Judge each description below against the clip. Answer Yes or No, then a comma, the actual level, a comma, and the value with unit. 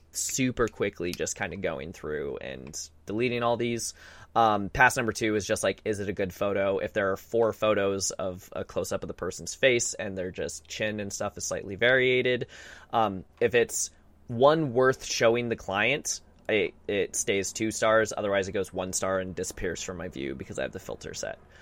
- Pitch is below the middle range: Yes, low, 110 Hz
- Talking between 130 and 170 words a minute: No, fast, 205 wpm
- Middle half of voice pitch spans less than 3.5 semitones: No, average, 3.8 semitones